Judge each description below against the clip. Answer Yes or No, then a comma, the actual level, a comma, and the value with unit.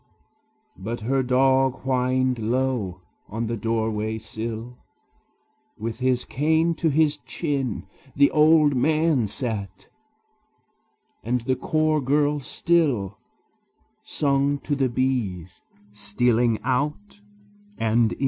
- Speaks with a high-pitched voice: No, low, 130 Hz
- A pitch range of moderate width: Yes, average, 4.2 semitones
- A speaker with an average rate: No, slow, 105 wpm